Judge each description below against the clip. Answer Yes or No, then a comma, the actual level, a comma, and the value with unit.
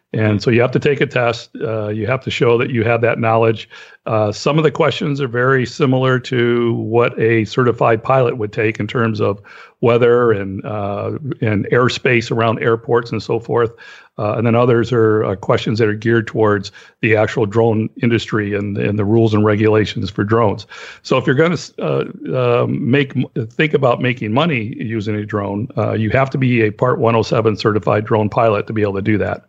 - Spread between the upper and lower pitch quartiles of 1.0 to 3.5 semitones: Yes, narrow, 2.4 semitones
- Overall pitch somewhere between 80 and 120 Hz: Yes, low, 115 Hz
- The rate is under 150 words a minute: No, fast, 205 wpm